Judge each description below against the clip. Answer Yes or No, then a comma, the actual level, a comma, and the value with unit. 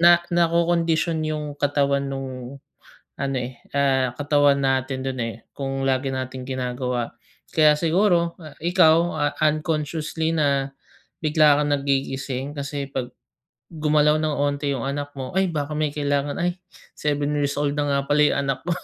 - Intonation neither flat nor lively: No, narrow, 2.3 semitones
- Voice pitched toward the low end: No, medium, 145 Hz